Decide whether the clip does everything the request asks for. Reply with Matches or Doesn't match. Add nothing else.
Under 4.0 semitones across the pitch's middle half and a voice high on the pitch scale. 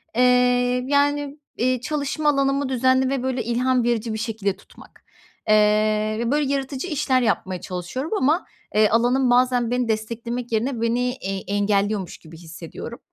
Matches